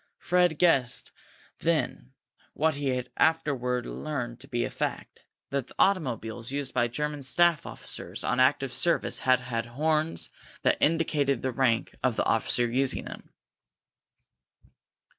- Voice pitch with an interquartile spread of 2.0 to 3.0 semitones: No, average, 3.8 semitones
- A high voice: No, low, 135 Hz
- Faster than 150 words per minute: No, slow, 135 wpm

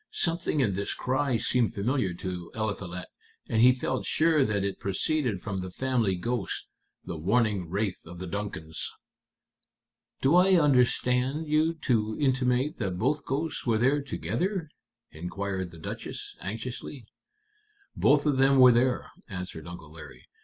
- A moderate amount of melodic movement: No, wide, 6.1 semitones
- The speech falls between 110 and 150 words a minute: Yes, average, 145 wpm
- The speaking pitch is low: Yes, low, 115 Hz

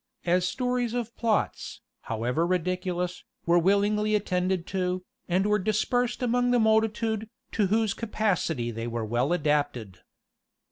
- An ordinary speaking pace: No, slow, 130 wpm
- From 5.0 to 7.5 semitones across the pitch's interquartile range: No, average, 4.4 semitones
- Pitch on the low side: No, high, 190 Hz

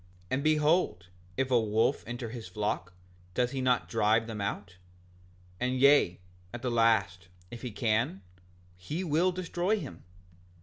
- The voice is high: No, low, 120 Hz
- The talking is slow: No, average, 145 wpm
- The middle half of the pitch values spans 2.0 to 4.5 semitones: No, average, 4.9 semitones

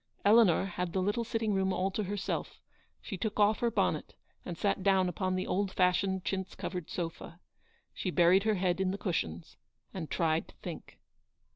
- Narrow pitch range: Yes, narrow, 2.2 semitones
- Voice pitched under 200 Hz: Yes, high, 190 Hz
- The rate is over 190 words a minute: No, average, 185 wpm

